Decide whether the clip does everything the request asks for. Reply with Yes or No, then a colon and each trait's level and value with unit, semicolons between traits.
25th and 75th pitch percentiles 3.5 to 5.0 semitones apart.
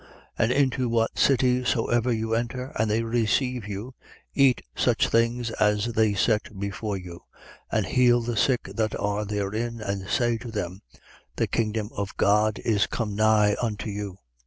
No: narrow, 2.5 semitones